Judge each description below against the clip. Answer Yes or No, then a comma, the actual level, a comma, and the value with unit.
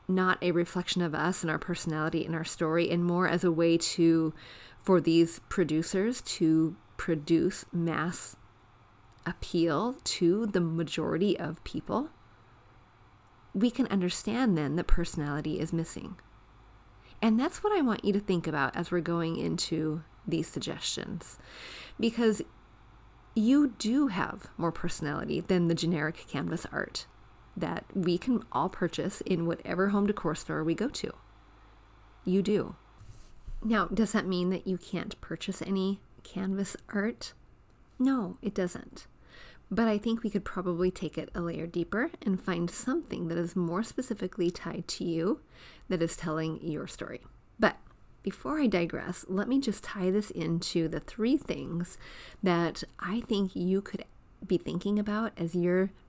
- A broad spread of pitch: No, average, 3.7 semitones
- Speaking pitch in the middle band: Yes, medium, 175 Hz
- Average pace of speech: Yes, average, 150 wpm